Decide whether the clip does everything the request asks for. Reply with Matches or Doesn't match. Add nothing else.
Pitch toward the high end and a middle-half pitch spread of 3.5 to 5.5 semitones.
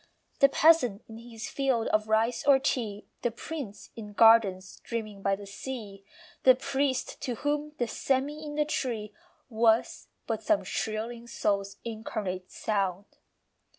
Matches